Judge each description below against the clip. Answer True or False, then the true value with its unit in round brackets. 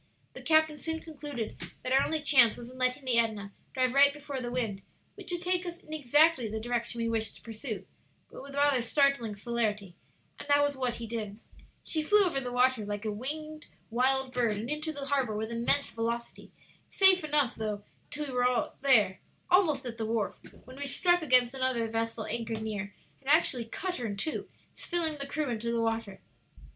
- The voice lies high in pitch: True (255 Hz)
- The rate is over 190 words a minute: True (200 wpm)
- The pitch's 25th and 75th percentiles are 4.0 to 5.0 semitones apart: True (4.3 semitones)